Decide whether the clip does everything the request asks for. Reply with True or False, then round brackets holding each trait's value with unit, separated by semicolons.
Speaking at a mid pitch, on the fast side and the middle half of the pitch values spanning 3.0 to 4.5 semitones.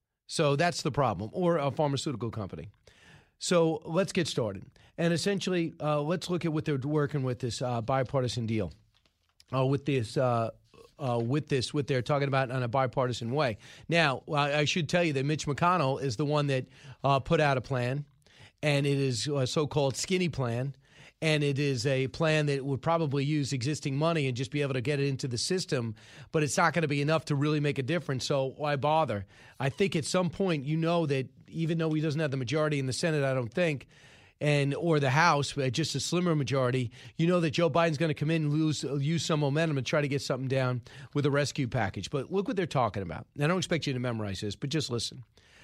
True (145 Hz; 225 wpm; 3.4 semitones)